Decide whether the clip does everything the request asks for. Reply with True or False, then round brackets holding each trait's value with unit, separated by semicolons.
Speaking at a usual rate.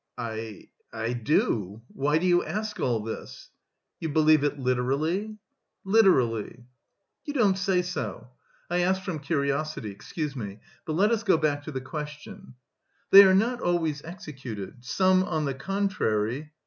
True (150 wpm)